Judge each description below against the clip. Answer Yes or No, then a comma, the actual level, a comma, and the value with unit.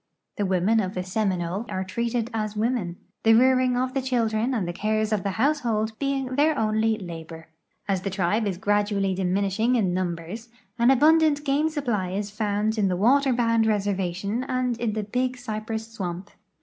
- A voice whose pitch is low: No, high, 215 Hz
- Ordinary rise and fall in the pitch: Yes, average, 4.2 semitones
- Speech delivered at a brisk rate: No, average, 180 wpm